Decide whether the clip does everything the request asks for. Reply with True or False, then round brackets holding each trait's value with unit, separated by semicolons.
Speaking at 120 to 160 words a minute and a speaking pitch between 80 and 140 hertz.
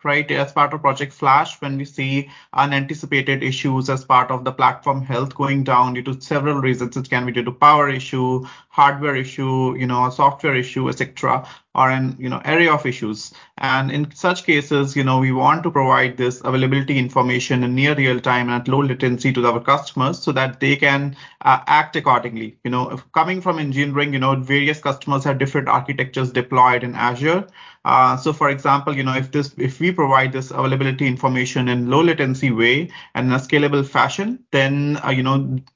False (200 wpm; 135 Hz)